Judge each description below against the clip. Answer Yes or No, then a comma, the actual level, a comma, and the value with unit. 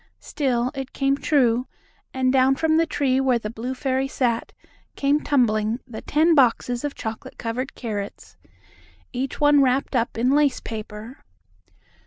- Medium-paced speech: Yes, average, 150 wpm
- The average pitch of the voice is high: Yes, very high, 260 Hz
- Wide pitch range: No, average, 3.1 semitones